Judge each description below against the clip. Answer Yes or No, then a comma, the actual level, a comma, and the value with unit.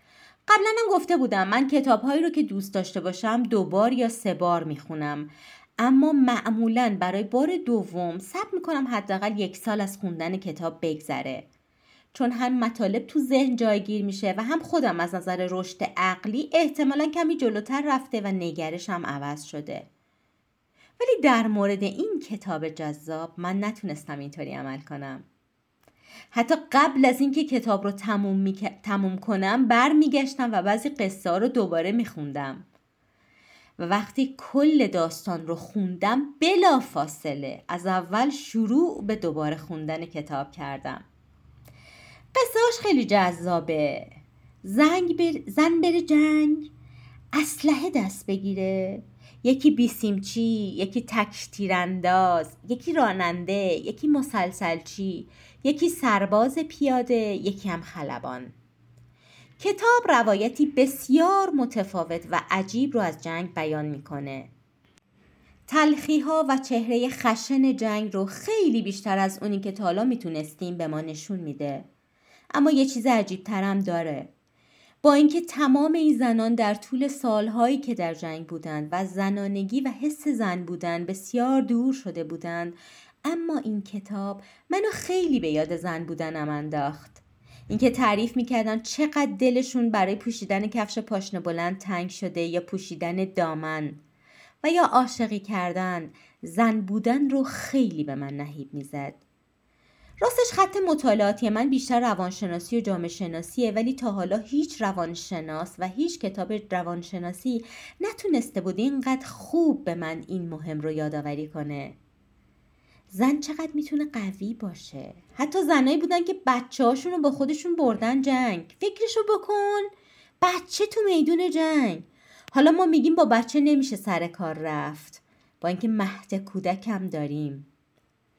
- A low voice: No, high, 210 Hz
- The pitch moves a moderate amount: No, wide, 7.8 semitones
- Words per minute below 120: No, average, 130 wpm